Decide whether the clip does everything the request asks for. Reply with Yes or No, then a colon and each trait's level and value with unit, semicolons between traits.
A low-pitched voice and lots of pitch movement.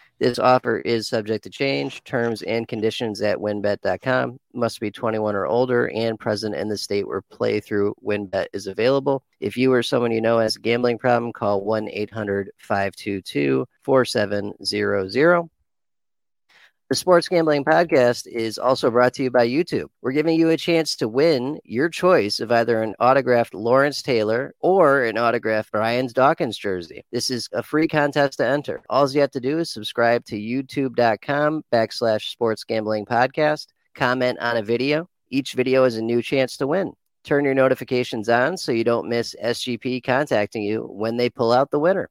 No: low, 120 Hz; average, 3.4 semitones